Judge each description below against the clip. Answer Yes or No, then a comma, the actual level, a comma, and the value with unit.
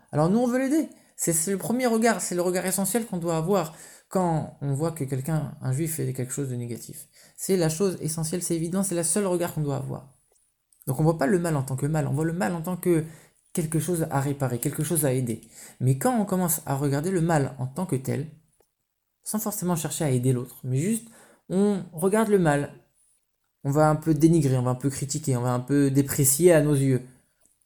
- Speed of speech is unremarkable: No, fast, 240 wpm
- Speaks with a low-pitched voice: No, medium, 160 Hz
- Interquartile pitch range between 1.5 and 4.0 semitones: No, average, 4.7 semitones